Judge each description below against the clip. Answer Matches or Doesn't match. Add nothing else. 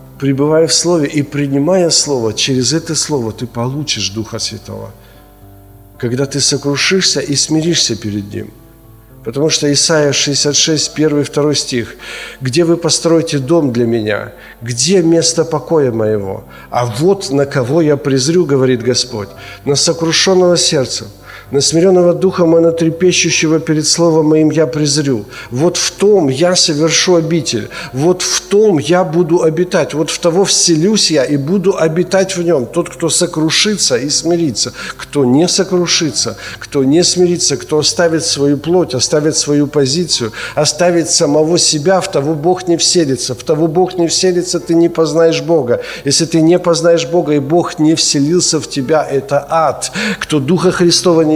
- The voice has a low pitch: Doesn't match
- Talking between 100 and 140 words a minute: Doesn't match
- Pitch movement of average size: Matches